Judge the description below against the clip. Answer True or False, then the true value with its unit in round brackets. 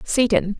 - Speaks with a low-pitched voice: False (215 Hz)